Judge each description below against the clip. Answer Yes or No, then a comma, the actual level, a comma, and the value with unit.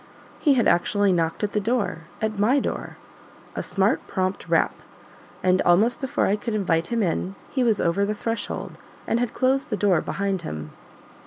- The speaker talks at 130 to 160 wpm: No, average, 180 wpm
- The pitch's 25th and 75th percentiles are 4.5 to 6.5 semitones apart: No, average, 3.9 semitones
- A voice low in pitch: No, high, 205 Hz